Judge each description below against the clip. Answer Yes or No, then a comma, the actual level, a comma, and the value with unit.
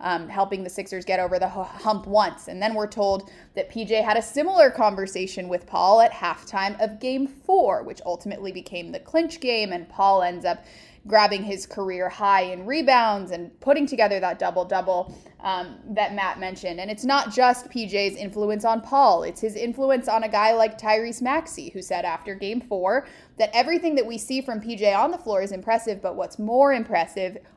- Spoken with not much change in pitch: No, average, 4.4 semitones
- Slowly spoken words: No, average, 200 wpm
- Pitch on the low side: No, high, 210 Hz